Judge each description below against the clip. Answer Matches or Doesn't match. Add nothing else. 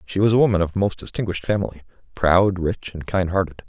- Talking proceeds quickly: Matches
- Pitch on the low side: Matches